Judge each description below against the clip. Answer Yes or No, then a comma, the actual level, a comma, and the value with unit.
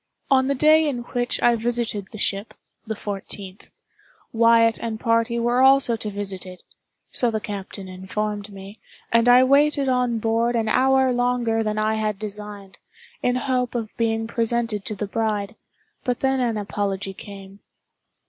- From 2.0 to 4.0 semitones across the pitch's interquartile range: Yes, average, 2.9 semitones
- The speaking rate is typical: Yes, average, 155 wpm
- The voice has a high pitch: Yes, high, 225 Hz